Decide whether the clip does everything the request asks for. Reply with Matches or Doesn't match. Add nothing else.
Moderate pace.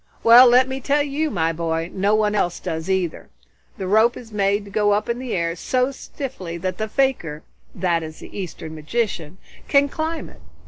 Matches